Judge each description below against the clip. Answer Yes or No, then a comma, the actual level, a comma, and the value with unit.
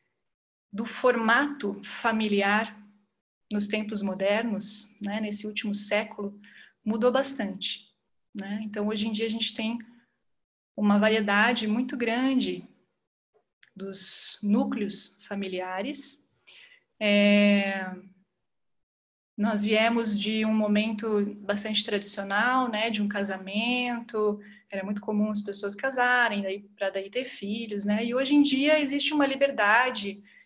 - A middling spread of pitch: No, narrow, 2.3 semitones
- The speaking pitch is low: No, high, 215 Hz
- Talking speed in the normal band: No, slow, 110 wpm